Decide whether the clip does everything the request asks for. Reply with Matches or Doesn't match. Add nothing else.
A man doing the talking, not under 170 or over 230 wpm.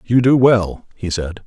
Matches